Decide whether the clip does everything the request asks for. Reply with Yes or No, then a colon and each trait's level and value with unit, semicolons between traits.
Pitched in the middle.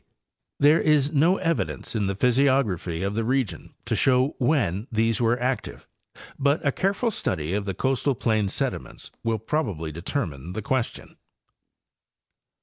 No: low, 120 Hz